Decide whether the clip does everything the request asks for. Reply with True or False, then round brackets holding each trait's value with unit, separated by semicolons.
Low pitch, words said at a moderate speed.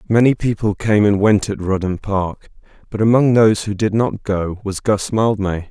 True (105 Hz; 190 wpm)